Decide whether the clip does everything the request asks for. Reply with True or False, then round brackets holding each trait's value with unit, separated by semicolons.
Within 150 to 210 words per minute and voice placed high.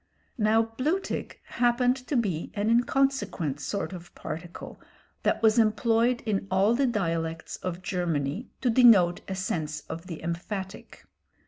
False (135 wpm; 200 Hz)